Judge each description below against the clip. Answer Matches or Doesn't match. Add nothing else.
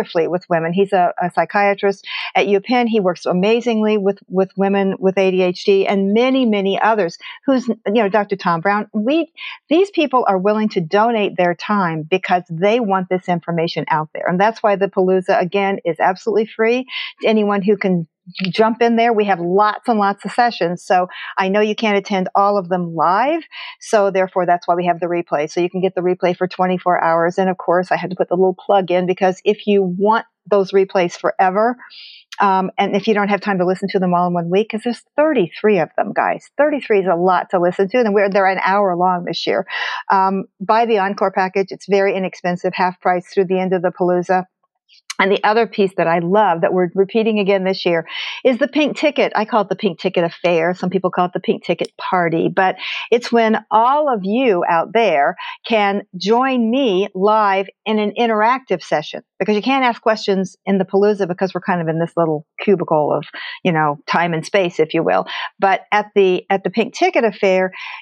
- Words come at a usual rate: Doesn't match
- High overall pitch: Matches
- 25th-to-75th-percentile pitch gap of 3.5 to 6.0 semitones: Doesn't match